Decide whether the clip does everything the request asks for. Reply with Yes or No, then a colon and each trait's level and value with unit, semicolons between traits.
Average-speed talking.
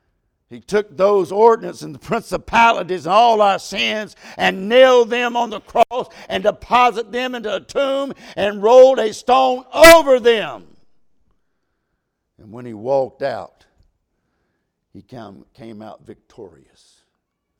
No: slow, 130 wpm